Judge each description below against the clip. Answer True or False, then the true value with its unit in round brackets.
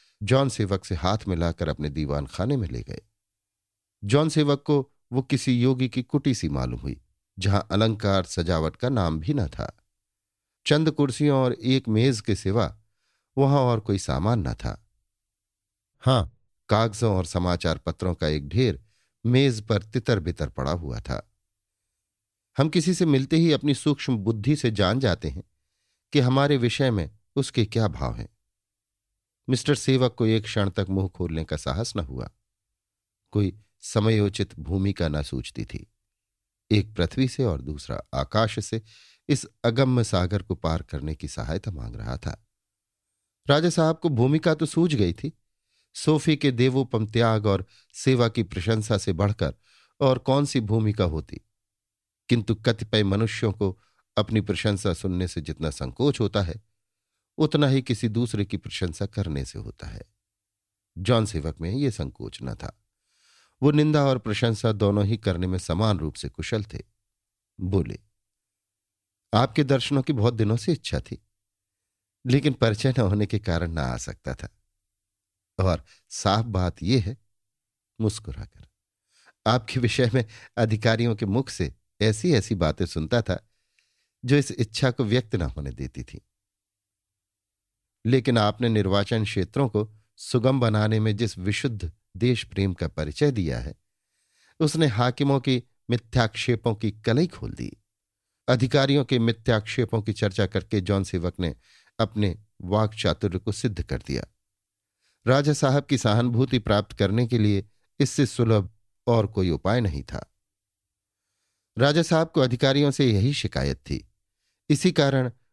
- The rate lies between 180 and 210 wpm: False (150 wpm)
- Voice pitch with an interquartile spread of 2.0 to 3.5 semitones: False (4.2 semitones)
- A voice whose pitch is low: True (105 Hz)